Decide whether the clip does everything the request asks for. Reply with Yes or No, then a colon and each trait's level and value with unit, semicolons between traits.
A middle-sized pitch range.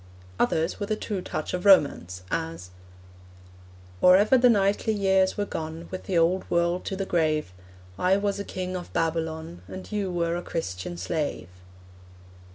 Yes: average, 3.5 semitones